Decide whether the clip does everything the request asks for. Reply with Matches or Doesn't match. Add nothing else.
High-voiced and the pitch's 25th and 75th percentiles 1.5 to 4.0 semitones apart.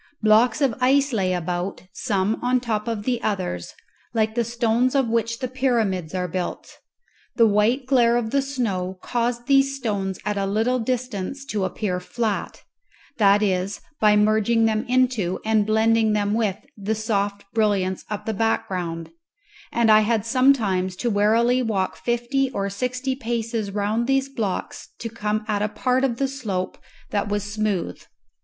Matches